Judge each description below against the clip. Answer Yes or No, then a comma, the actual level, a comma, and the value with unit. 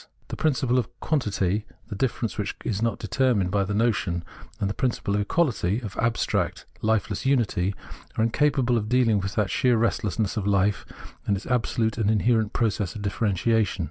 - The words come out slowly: No, average, 175 wpm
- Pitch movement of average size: Yes, average, 3.1 semitones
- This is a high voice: No, low, 110 Hz